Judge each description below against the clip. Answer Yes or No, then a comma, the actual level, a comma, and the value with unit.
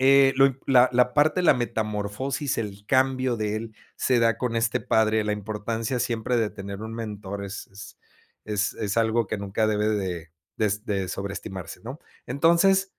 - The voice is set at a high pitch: No, low, 110 Hz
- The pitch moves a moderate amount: Yes, average, 3.6 semitones